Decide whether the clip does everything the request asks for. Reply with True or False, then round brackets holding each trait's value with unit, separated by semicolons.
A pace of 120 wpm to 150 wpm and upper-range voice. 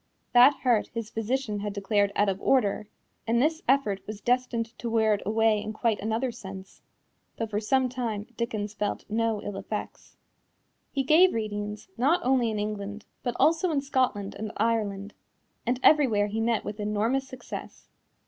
False (165 wpm; 225 Hz)